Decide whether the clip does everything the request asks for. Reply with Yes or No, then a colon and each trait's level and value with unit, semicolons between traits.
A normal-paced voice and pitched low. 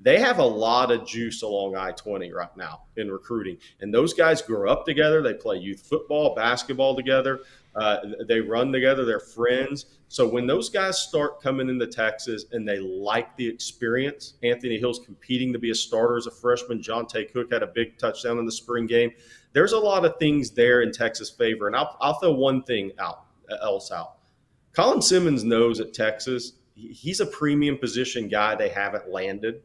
Yes: average, 195 wpm; low, 120 Hz